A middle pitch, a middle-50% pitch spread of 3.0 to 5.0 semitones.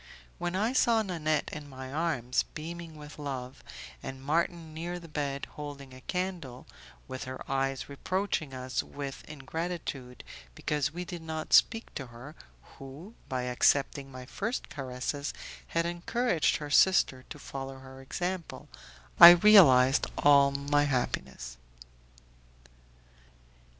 Yes: medium, 145 Hz; average, 4.4 semitones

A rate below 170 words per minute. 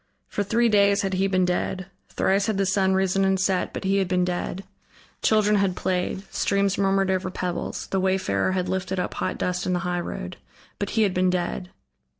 No: average, 200 wpm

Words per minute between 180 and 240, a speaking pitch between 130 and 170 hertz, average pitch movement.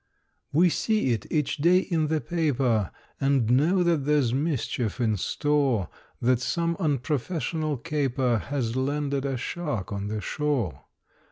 No: average, 140 wpm; medium, 140 Hz; average, 4.4 semitones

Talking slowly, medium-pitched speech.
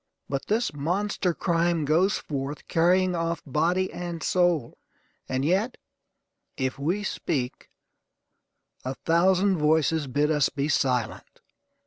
Yes: slow, 115 wpm; medium, 165 Hz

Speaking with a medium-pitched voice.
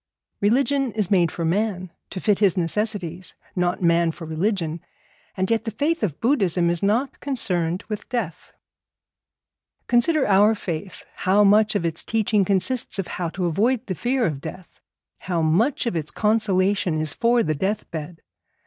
No: high, 195 Hz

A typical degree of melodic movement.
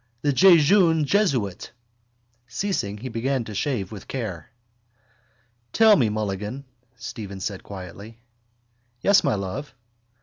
No: wide, 6.6 semitones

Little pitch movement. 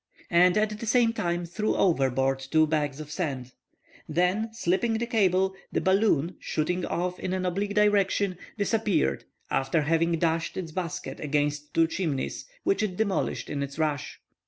No: average, 4.8 semitones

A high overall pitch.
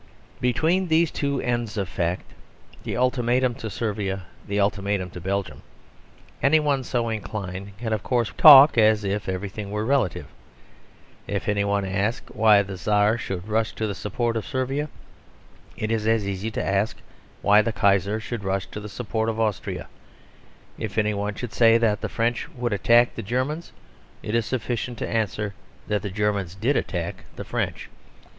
No: low, 110 Hz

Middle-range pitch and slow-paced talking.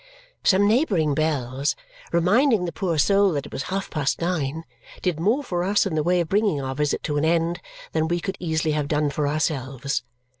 No: medium, 160 Hz; average, 200 wpm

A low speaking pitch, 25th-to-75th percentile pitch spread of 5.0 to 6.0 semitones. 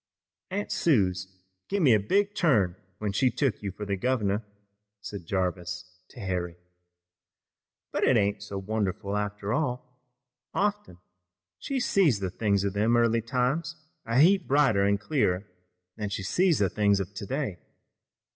Yes: low, 105 Hz; wide, 5.5 semitones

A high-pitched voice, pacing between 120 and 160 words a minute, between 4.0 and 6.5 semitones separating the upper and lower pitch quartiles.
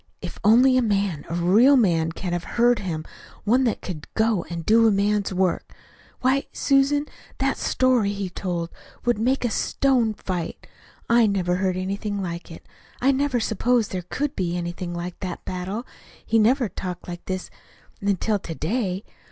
No: high, 200 Hz; average, 175 wpm; average, 5.1 semitones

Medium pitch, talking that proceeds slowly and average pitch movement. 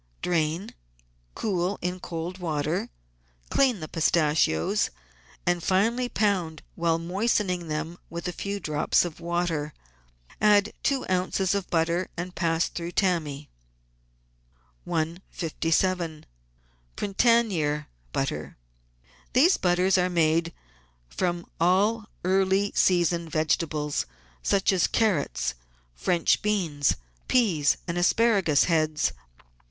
Yes: medium, 175 Hz; slow, 100 wpm; average, 3.2 semitones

